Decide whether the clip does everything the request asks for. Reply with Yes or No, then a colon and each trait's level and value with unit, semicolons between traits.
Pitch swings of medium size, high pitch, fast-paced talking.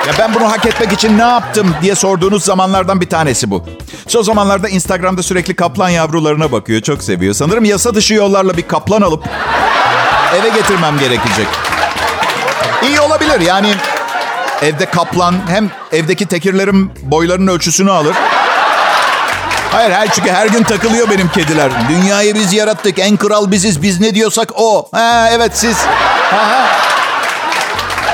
Yes: average, 4.1 semitones; high, 195 Hz; fast, 145 wpm